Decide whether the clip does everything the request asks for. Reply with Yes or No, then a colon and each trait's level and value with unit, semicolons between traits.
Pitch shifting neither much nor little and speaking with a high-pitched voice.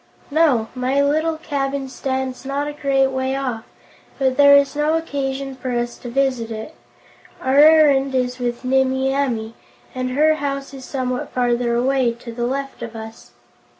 No: narrow, 2.1 semitones; very high, 265 Hz